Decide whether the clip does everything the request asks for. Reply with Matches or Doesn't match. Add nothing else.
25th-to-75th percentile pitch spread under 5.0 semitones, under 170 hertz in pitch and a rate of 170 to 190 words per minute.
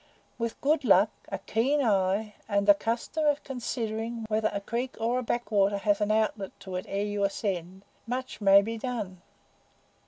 Doesn't match